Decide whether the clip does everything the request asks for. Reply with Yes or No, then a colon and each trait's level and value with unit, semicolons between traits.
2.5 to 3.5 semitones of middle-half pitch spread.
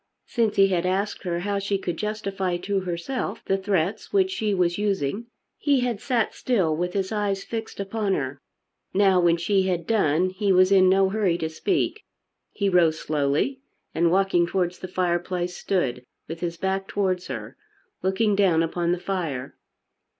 Yes: average, 2.8 semitones